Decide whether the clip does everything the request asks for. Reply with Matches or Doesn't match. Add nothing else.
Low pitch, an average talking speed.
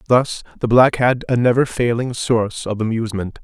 Matches